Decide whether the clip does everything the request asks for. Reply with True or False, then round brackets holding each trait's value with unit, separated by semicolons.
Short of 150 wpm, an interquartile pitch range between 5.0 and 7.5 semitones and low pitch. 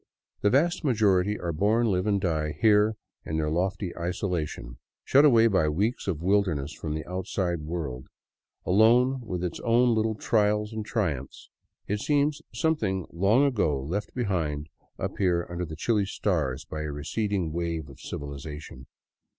False (155 wpm; 5.6 semitones; 95 Hz)